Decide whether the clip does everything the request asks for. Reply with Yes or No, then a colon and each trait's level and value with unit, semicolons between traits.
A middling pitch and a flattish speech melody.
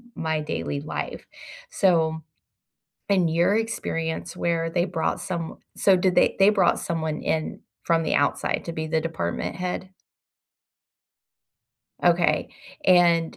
Yes: medium, 165 Hz; narrow, 2.3 semitones